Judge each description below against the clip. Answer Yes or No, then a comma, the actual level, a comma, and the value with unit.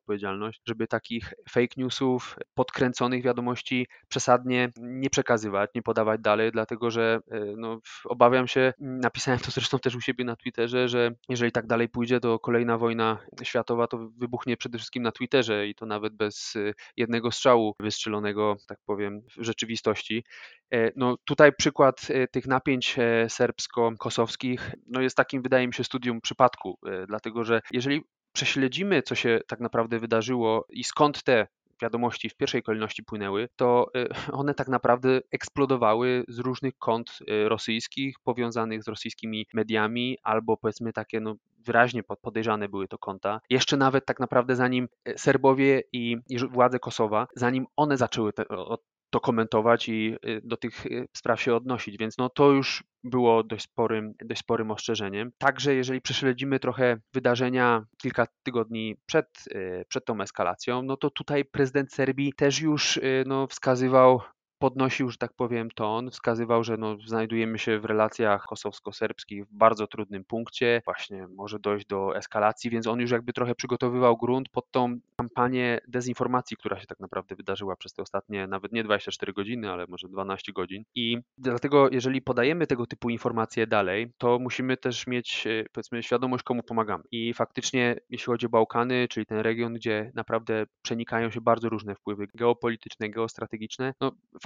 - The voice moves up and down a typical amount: No, narrow, 2.2 semitones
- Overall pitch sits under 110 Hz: No, low, 120 Hz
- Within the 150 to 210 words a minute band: Yes, average, 155 wpm